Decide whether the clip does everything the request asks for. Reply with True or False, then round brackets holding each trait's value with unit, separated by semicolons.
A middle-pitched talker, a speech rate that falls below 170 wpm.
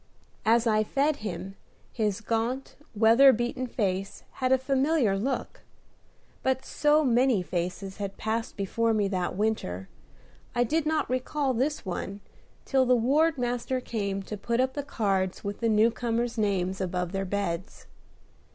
False (225 Hz; 155 wpm)